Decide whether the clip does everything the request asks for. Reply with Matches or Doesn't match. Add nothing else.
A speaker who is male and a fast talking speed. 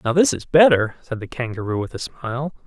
Matches